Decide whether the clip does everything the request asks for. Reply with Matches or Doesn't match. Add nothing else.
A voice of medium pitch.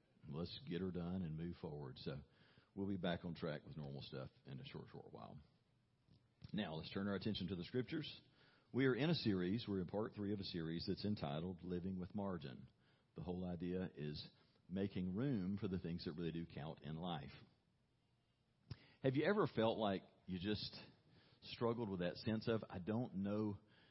Doesn't match